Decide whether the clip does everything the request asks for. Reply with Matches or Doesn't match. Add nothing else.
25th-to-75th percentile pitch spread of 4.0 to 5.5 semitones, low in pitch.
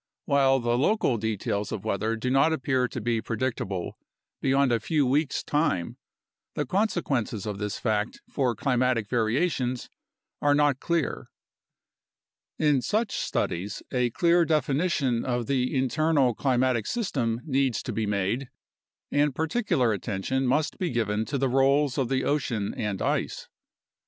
Matches